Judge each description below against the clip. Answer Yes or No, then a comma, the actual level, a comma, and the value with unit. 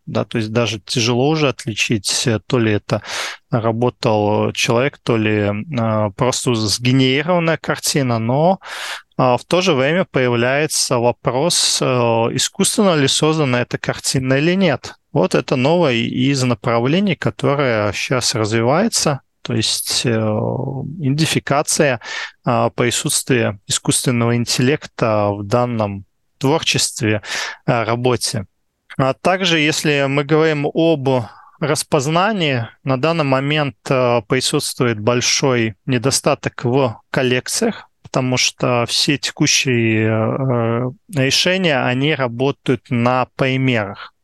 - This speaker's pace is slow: Yes, slow, 105 wpm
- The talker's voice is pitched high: No, low, 130 Hz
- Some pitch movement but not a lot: Yes, average, 4.1 semitones